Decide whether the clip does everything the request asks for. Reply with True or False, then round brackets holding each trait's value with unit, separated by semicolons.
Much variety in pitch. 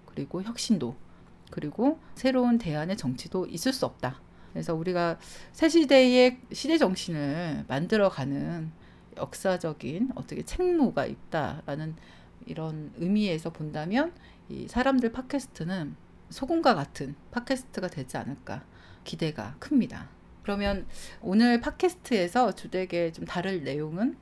True (8.1 semitones)